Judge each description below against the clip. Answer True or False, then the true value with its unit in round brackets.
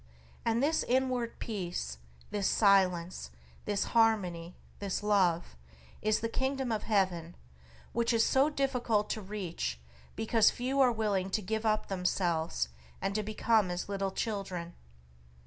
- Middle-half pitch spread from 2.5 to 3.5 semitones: False (4.0 semitones)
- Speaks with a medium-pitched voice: False (210 Hz)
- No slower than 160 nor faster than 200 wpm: False (135 wpm)